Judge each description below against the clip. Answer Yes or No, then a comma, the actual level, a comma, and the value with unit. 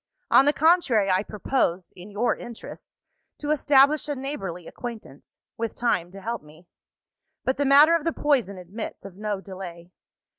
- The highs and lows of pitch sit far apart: Yes, wide, 6.8 semitones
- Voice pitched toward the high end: Yes, high, 225 Hz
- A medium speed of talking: Yes, average, 160 wpm